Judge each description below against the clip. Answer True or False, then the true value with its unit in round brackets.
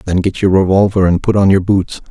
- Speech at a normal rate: False (255 wpm)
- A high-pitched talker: False (95 Hz)